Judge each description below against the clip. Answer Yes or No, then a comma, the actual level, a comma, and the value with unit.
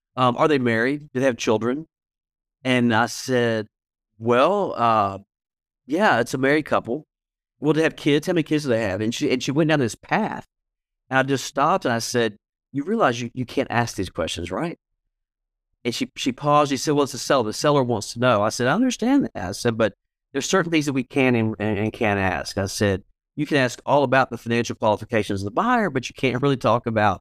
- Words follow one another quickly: Yes, fast, 230 wpm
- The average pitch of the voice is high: No, low, 125 Hz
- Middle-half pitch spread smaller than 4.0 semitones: No, average, 4.4 semitones